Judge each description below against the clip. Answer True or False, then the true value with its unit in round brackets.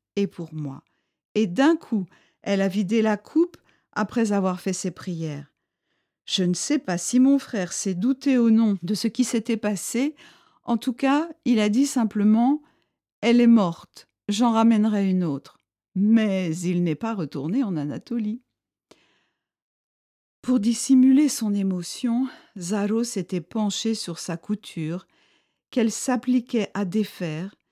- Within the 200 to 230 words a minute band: False (145 wpm)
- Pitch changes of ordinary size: True (4.7 semitones)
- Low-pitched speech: False (215 Hz)